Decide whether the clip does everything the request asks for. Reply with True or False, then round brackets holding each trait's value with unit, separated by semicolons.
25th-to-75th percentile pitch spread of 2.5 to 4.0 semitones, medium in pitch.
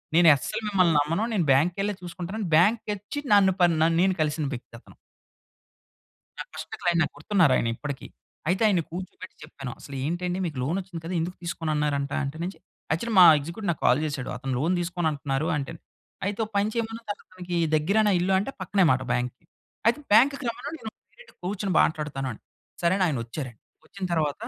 False (4.7 semitones; 170 Hz)